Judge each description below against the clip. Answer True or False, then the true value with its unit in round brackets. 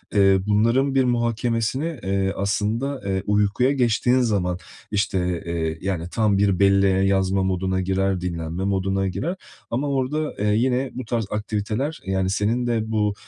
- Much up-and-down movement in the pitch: False (3.9 semitones)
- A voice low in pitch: True (105 Hz)